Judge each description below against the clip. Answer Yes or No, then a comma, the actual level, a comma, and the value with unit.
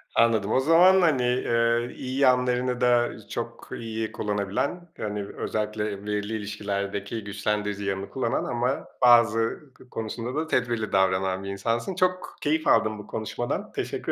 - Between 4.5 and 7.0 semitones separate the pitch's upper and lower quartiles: No, average, 3.4 semitones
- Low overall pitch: Yes, low, 115 Hz